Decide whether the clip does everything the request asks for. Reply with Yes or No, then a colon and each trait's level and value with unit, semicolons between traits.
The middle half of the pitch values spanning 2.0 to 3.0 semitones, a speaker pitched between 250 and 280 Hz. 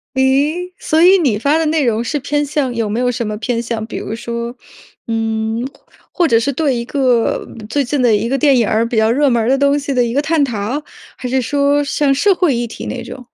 No: average, 3.8 semitones; very high, 255 Hz